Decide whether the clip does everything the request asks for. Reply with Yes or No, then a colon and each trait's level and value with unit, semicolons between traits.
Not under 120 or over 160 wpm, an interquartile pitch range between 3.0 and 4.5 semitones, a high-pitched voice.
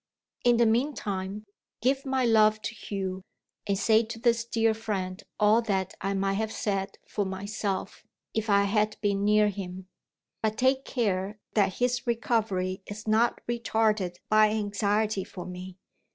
No: average, 150 wpm; narrow, 2.5 semitones; high, 210 Hz